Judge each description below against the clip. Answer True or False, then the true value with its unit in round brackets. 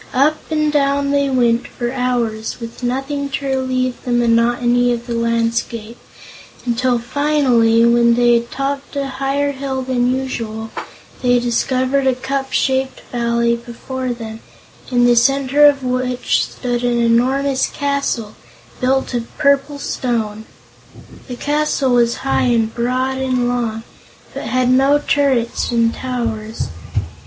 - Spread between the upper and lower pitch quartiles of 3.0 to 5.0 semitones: False (2.4 semitones)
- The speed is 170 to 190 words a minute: False (135 wpm)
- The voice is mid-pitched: False (250 Hz)